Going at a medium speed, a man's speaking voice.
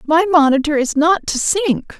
No: average, 180 wpm; female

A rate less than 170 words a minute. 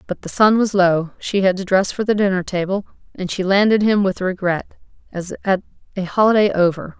No: fast, 205 wpm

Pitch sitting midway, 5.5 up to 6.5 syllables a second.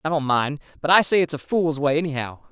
Yes: medium, 145 Hz; 5.9 syllables/s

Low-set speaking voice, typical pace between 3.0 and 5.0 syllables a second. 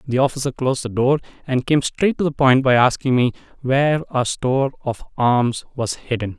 No: low, 130 Hz; 5.2 syllables/s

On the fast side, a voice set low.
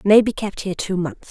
No: fast, 275 wpm; high, 195 Hz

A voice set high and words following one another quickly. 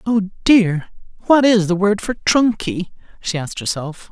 No: high, 200 Hz; average, 175 wpm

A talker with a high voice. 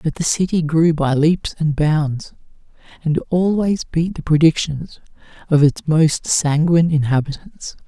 No: medium, 160 Hz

